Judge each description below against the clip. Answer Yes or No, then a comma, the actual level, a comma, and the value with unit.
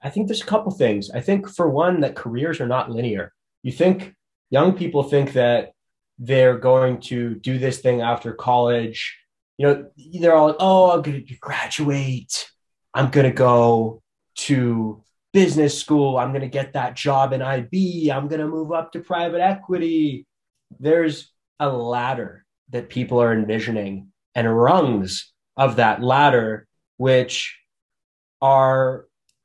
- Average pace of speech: Yes, average, 145 wpm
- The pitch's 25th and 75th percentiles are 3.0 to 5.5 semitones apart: Yes, average, 4.7 semitones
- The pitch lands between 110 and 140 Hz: Yes, low, 135 Hz